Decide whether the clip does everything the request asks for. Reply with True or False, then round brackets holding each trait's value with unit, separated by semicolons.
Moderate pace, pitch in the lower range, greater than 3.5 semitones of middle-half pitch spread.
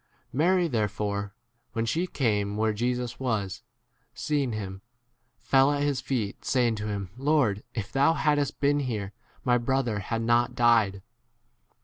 True (145 wpm; 120 Hz; 4.6 semitones)